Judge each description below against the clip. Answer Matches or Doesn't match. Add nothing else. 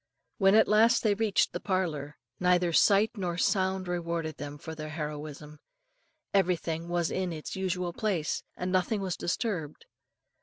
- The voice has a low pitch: Doesn't match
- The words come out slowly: Doesn't match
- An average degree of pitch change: Matches